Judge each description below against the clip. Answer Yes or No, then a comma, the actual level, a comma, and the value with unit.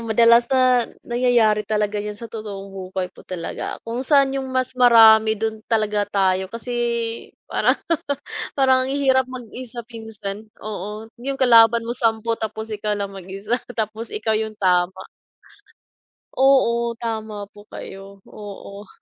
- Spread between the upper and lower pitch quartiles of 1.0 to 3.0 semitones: Yes, average, 2.7 semitones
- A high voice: Yes, high, 220 Hz